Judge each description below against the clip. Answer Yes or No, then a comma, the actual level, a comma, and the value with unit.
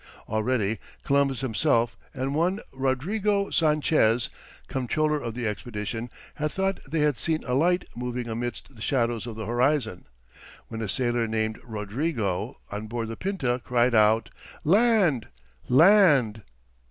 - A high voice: No, low, 125 Hz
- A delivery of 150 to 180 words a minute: No, slow, 135 wpm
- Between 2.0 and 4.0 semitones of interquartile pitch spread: No, average, 5.3 semitones